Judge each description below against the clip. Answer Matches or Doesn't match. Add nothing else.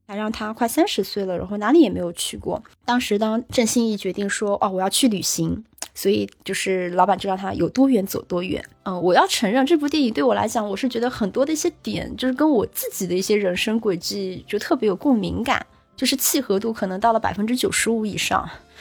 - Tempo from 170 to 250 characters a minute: Doesn't match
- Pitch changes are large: Doesn't match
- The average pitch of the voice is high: Matches